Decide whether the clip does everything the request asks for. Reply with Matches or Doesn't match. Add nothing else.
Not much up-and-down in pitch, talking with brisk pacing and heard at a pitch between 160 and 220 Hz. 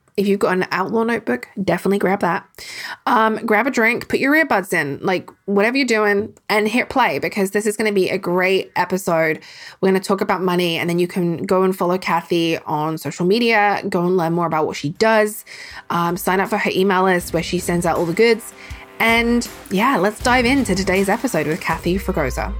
Doesn't match